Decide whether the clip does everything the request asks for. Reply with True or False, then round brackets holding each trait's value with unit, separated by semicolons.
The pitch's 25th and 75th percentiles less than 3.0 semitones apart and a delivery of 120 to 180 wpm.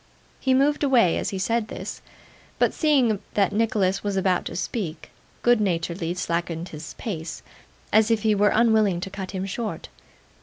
False (4.0 semitones; 165 wpm)